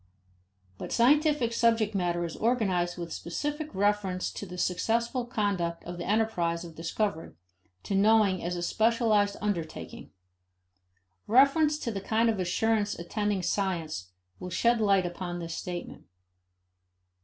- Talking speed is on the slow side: Yes, slow, 130 wpm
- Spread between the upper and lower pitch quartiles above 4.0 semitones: Yes, average, 4.5 semitones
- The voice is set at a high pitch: Yes, high, 200 Hz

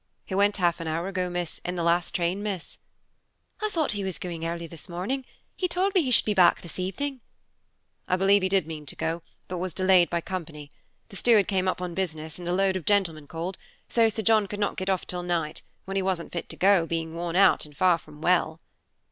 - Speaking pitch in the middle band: Yes, medium, 180 Hz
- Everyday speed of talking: No, fast, 230 wpm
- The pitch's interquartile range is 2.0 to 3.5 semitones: Yes, average, 2.7 semitones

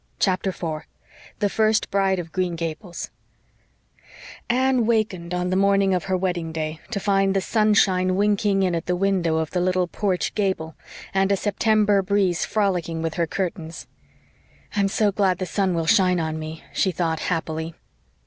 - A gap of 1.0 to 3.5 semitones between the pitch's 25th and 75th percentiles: Yes, average, 2.9 semitones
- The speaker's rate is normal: Yes, average, 170 wpm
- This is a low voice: No, medium, 185 Hz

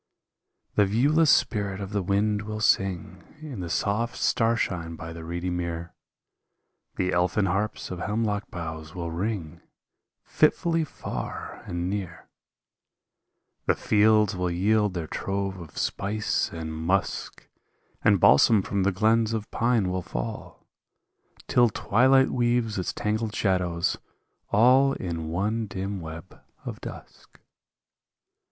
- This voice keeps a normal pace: No, slow, 125 wpm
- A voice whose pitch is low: Yes, low, 100 Hz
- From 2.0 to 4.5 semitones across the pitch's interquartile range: Yes, average, 3.9 semitones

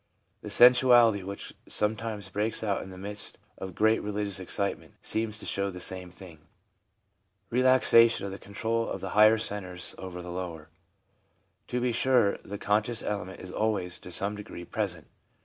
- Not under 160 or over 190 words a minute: Yes, average, 165 wpm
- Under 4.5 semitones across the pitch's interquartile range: Yes, average, 3.1 semitones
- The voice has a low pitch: Yes, low, 100 Hz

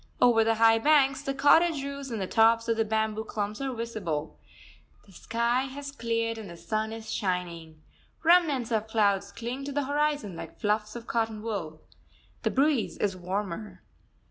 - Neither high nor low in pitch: No, high, 225 Hz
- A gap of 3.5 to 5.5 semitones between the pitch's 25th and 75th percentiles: Yes, average, 4.2 semitones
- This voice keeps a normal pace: Yes, average, 170 wpm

